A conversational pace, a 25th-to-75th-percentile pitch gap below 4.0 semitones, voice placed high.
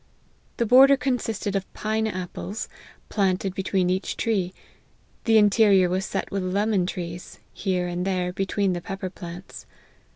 Yes: average, 155 wpm; average, 2.7 semitones; high, 195 Hz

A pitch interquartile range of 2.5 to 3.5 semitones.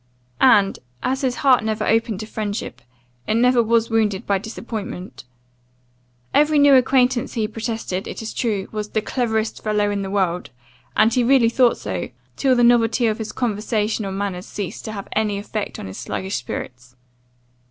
Yes: average, 2.8 semitones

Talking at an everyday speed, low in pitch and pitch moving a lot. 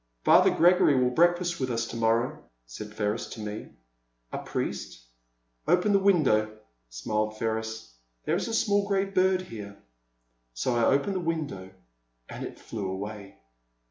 Yes: average, 150 wpm; low, 120 Hz; wide, 8.6 semitones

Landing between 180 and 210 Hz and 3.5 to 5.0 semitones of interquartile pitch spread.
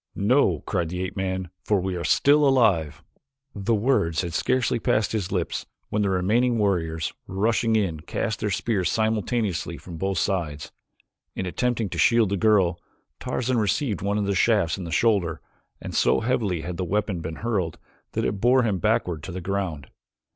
No: low, 100 Hz; average, 4.1 semitones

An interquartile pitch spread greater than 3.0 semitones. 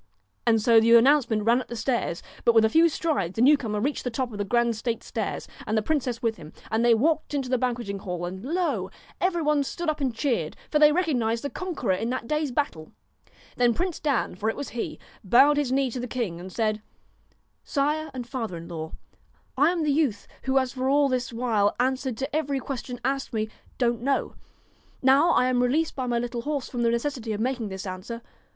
Yes: average, 4.1 semitones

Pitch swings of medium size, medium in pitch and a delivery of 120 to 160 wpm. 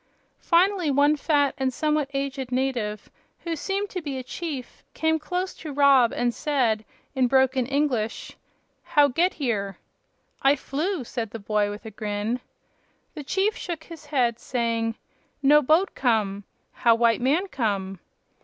No: average, 4.9 semitones; very high, 270 Hz; average, 150 wpm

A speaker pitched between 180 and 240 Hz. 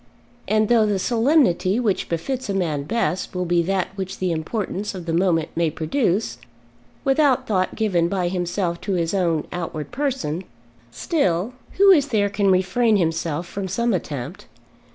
Yes: high, 190 Hz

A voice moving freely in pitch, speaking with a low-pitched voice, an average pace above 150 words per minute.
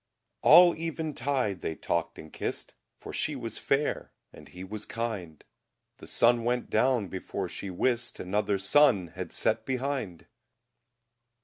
No: wide, 5.9 semitones; low, 115 Hz; average, 140 wpm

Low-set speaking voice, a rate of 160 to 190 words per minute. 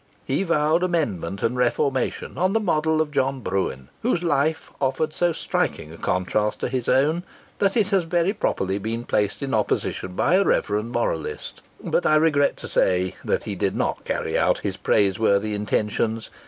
Yes: low, 130 Hz; average, 175 wpm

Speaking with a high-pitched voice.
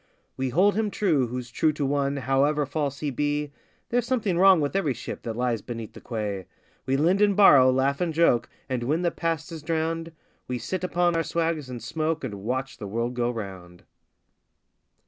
No: medium, 145 Hz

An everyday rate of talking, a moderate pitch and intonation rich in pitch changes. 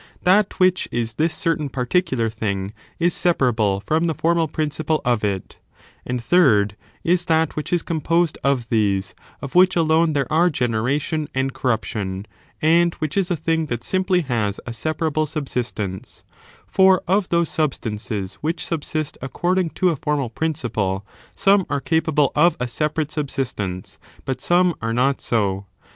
Yes: average, 155 wpm; medium, 150 Hz; wide, 6.4 semitones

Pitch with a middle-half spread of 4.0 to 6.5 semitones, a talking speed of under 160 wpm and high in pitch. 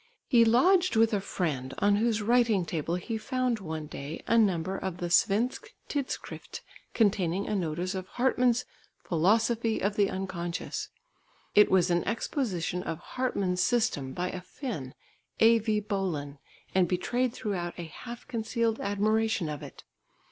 Yes: average, 4.7 semitones; average, 145 wpm; high, 200 Hz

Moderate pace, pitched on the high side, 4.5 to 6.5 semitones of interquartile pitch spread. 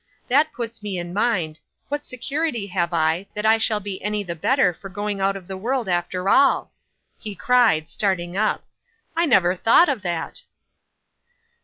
Yes: average, 170 wpm; high, 205 Hz; average, 4.9 semitones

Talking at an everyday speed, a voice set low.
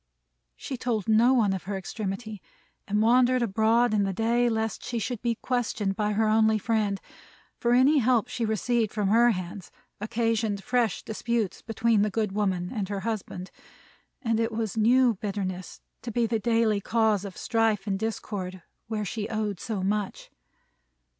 No: average, 165 wpm; high, 220 Hz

